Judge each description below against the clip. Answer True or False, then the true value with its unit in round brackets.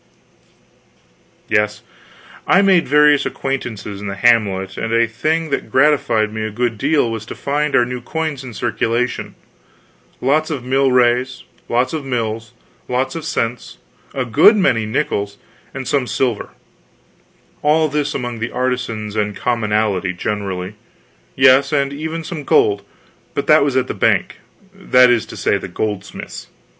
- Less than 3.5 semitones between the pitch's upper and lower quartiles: False (4.5 semitones)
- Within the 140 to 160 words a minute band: True (150 wpm)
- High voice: False (125 Hz)